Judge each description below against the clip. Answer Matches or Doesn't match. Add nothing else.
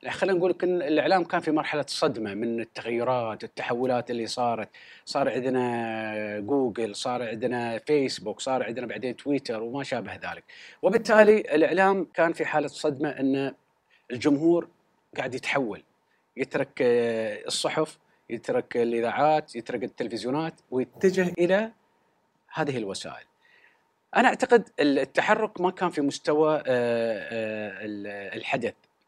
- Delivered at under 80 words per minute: Doesn't match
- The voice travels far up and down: Matches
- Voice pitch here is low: Doesn't match